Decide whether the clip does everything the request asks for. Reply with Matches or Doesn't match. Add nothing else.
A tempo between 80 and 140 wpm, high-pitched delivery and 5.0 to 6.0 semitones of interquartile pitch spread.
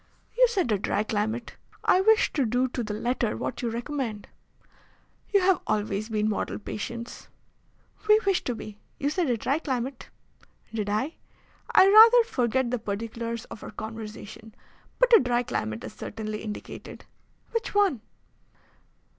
Doesn't match